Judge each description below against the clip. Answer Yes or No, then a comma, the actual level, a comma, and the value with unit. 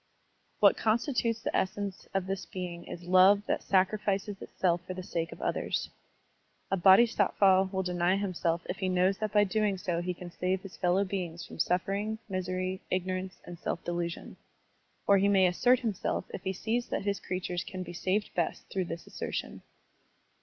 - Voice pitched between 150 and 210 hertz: Yes, medium, 185 Hz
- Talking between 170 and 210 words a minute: Yes, average, 180 wpm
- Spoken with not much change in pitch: Yes, narrow, 1.9 semitones